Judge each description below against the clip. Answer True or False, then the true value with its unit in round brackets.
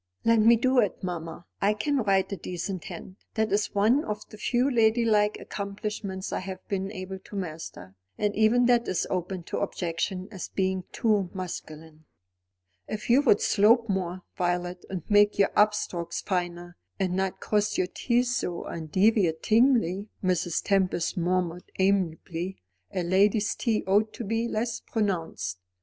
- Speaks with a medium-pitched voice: False (195 Hz)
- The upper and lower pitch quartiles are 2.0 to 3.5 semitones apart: True (3.2 semitones)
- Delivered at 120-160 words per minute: True (155 wpm)